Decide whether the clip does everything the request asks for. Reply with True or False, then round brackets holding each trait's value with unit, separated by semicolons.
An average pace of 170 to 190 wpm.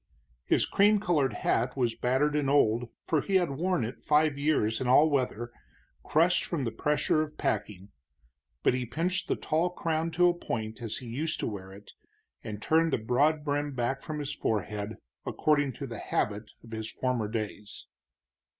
True (180 wpm)